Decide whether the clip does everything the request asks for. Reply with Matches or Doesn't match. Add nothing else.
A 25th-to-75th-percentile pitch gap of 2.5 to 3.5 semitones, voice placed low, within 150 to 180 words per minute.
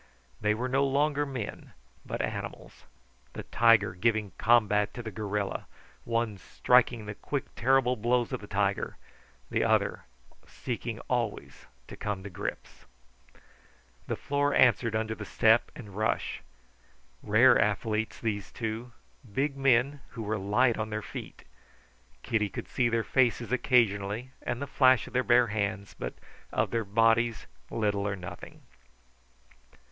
Doesn't match